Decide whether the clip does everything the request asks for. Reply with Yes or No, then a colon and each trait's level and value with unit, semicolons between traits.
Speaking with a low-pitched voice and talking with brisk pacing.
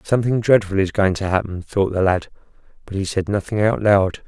Yes: low, 100 Hz; fast, 210 wpm